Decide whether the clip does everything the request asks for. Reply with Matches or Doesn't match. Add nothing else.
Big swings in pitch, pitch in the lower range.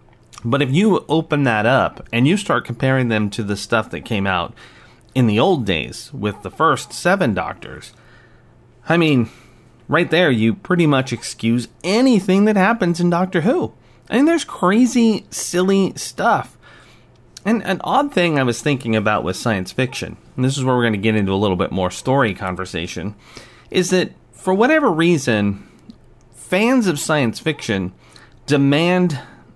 Matches